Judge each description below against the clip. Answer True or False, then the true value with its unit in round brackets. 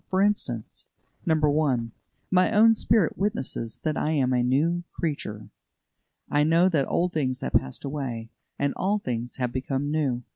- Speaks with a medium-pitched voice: True (145 Hz)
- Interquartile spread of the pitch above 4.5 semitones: True (5.5 semitones)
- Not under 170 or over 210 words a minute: False (155 wpm)